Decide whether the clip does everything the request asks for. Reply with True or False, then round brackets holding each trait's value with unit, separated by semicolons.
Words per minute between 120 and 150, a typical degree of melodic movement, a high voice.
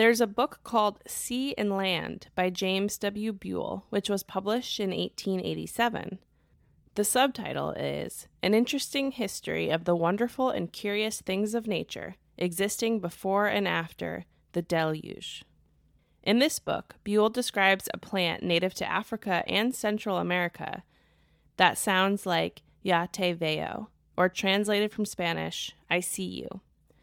True (135 wpm; 3.7 semitones; 200 Hz)